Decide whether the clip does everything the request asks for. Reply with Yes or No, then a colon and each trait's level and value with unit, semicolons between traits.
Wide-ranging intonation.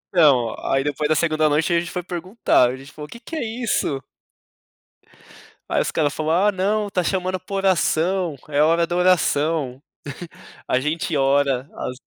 No: average, 4.3 semitones